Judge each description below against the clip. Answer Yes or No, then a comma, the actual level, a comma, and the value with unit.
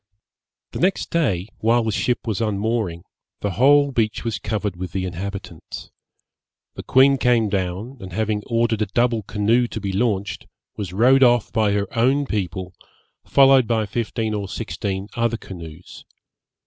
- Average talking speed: Yes, average, 155 wpm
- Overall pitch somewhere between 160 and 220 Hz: No, low, 110 Hz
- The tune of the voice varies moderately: Yes, average, 3.5 semitones